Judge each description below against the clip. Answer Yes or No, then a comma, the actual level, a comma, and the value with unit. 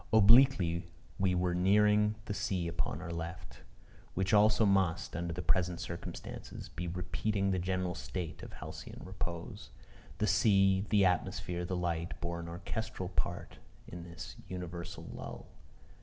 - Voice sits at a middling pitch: No, very low, 90 Hz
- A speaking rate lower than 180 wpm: Yes, average, 140 wpm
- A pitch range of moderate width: No, narrow, 2.3 semitones